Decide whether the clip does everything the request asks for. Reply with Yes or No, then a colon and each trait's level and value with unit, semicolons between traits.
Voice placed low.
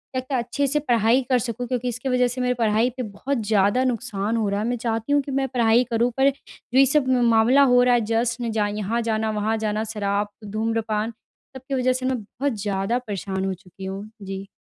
No: high, 230 Hz